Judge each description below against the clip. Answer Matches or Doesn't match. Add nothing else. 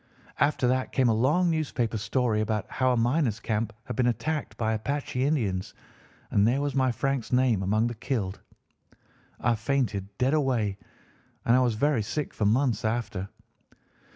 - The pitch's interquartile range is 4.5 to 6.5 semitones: Doesn't match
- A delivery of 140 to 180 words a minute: Matches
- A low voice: Matches